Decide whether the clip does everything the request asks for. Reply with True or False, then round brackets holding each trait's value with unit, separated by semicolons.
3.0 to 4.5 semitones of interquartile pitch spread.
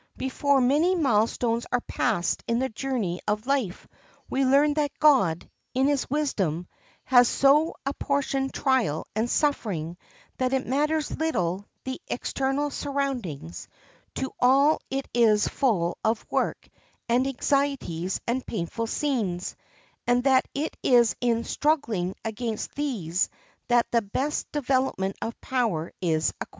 False (4.9 semitones)